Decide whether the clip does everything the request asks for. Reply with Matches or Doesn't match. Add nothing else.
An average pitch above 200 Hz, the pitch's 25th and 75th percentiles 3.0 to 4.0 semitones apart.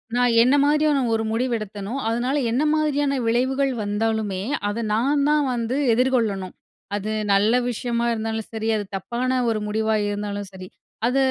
Matches